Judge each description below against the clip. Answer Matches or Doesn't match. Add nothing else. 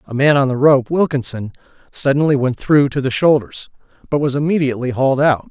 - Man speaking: Matches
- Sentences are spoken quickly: Doesn't match